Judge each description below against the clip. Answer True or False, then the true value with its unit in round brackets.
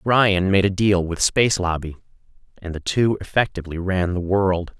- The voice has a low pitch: True (95 Hz)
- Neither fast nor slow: True (175 wpm)